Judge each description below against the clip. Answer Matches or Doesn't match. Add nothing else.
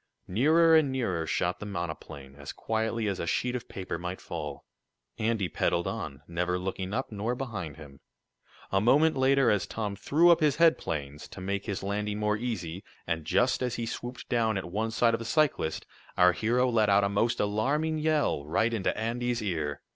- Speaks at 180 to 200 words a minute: Matches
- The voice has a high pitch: Doesn't match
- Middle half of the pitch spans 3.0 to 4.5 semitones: Doesn't match